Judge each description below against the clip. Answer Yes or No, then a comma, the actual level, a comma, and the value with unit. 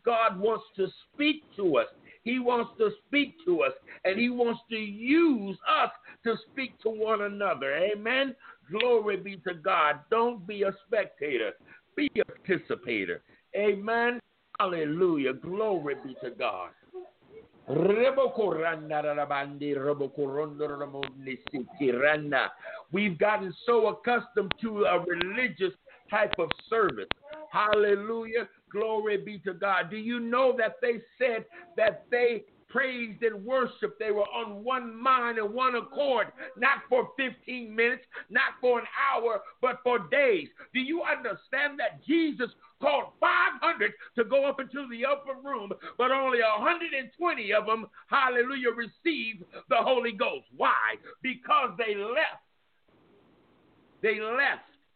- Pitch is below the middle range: No, high, 235 Hz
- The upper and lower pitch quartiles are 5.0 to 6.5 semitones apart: No, average, 4.5 semitones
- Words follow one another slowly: Yes, slow, 125 wpm